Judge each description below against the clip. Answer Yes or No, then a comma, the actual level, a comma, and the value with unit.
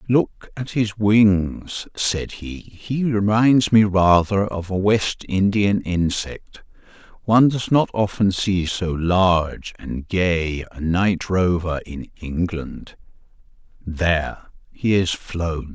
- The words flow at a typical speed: No, slow, 125 wpm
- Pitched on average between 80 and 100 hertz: Yes, very low, 95 Hz